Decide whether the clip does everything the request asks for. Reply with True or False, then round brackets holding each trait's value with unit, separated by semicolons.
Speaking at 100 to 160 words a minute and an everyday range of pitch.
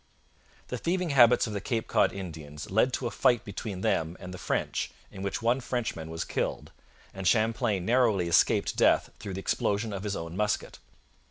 False (185 wpm; 4.5 semitones)